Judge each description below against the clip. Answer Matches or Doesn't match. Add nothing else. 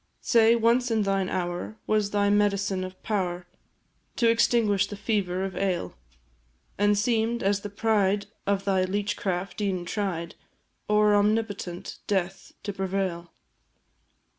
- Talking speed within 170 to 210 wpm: Doesn't match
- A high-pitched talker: Matches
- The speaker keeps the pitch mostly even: Matches